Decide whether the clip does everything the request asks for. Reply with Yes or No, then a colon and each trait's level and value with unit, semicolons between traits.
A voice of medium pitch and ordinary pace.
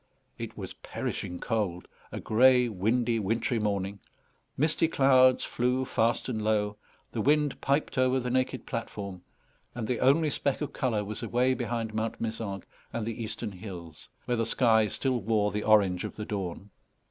No: low, 115 Hz; average, 165 wpm